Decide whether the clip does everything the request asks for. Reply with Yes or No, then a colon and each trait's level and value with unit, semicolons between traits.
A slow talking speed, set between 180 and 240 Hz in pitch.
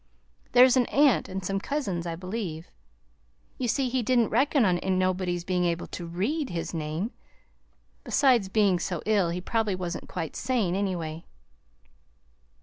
No: average, 145 wpm; high, 190 Hz